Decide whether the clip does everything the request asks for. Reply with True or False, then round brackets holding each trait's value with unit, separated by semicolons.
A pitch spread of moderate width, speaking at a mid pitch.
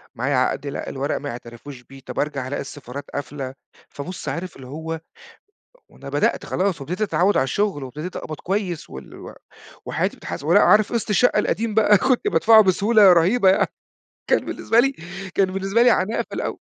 False (6.8 semitones; 180 Hz)